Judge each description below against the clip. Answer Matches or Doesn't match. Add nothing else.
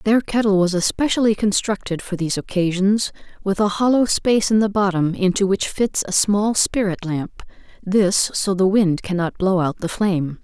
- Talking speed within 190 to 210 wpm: Doesn't match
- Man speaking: Doesn't match